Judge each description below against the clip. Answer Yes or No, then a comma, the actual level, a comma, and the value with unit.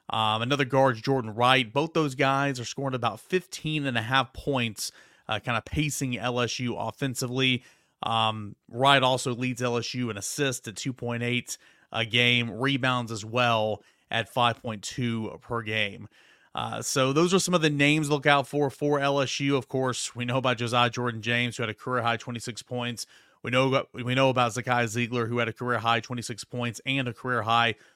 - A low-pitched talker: Yes, low, 125 Hz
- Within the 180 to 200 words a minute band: Yes, average, 190 wpm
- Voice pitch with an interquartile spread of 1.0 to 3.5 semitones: Yes, narrow, 2.4 semitones